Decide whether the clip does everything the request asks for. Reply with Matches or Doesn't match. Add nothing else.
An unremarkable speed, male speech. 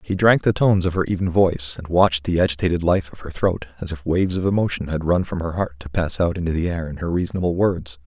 Doesn't match